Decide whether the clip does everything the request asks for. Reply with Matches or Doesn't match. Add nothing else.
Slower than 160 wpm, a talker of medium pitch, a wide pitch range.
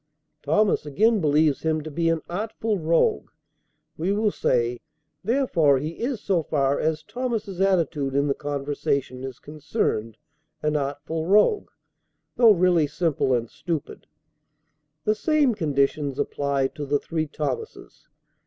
Matches